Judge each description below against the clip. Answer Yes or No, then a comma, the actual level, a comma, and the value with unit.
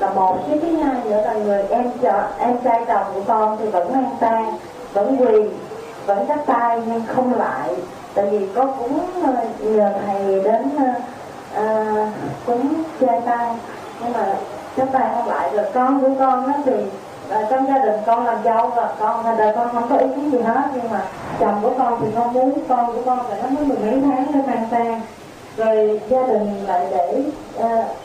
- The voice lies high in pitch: Yes, high, 235 Hz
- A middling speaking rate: Yes, average, 200 wpm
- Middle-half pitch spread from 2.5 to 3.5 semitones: Yes, average, 3.2 semitones